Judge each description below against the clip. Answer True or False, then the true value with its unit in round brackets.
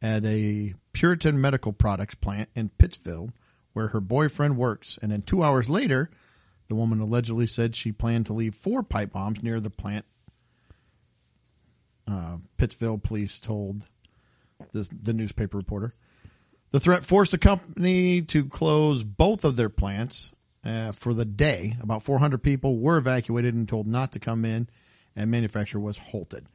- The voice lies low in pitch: True (115 Hz)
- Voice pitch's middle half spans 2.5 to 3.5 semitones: False (4.0 semitones)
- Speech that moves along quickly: False (155 wpm)